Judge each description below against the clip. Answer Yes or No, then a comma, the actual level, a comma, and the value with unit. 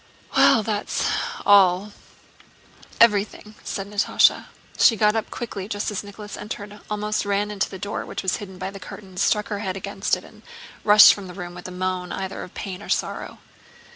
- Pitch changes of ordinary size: No, narrow, 1.8 semitones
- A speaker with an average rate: Yes, average, 175 wpm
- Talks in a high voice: Yes, high, 200 Hz